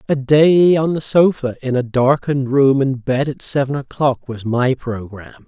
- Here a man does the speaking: Yes, male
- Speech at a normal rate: Yes, average, 185 wpm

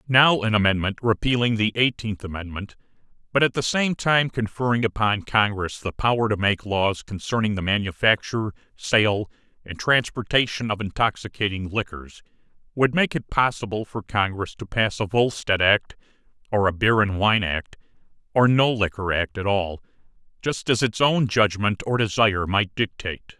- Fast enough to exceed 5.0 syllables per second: No, 4.9 syllables/s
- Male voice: Yes, male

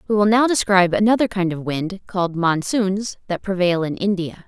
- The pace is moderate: Yes, average, 190 wpm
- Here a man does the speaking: No, female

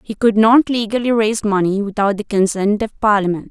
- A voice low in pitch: No, high, 210 Hz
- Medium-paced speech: Yes, average, 190 wpm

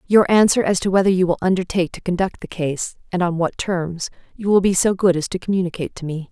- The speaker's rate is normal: No, fast, 245 wpm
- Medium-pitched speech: Yes, medium, 180 Hz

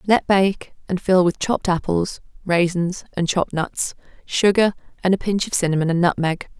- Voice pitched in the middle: Yes, medium, 180 Hz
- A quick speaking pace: No, average, 175 wpm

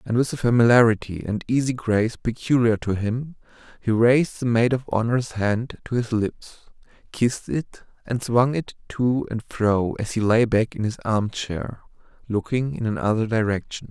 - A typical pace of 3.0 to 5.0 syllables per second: Yes, 4.8 syllables/s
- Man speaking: Yes, male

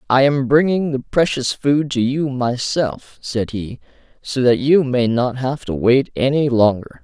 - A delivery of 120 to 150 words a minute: No, average, 180 wpm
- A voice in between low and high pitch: No, low, 130 Hz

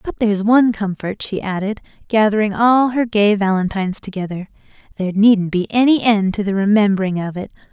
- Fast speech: No, average, 170 wpm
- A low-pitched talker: No, high, 205 Hz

